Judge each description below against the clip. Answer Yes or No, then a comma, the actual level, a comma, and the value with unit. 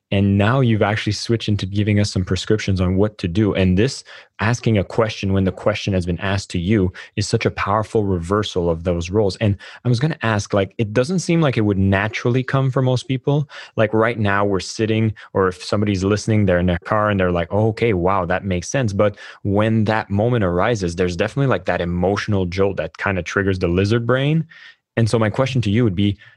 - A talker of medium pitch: No, low, 105 Hz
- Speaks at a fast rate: Yes, fast, 230 wpm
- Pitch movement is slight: No, average, 3.0 semitones